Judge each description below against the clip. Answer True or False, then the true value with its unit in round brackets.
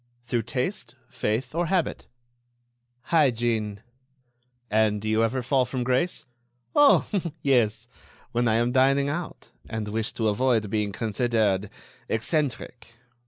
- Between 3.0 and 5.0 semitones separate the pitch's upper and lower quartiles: True (3.3 semitones)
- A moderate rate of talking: False (120 wpm)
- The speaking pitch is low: True (120 Hz)